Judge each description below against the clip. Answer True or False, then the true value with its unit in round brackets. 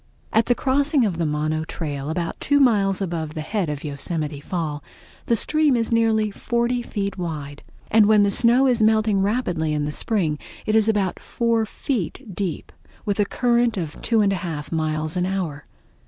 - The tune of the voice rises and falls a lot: True (6.4 semitones)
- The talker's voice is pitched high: True (195 Hz)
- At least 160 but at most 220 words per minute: True (190 wpm)